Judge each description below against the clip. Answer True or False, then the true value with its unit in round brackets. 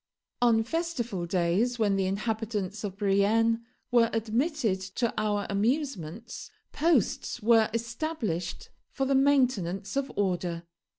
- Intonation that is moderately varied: True (3.9 semitones)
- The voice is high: True (220 Hz)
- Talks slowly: True (115 wpm)